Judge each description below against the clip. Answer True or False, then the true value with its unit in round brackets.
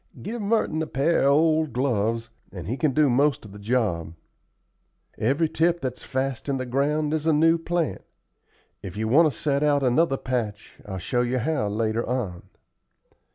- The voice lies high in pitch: False (135 Hz)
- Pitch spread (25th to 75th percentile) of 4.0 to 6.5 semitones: True (5.4 semitones)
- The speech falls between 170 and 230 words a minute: True (180 wpm)